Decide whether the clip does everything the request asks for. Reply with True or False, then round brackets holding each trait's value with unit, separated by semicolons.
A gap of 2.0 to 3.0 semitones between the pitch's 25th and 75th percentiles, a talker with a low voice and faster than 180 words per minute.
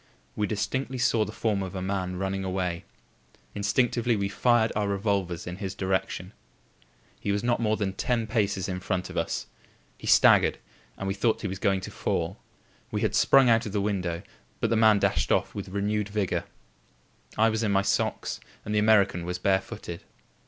True (2.4 semitones; 100 Hz; 190 wpm)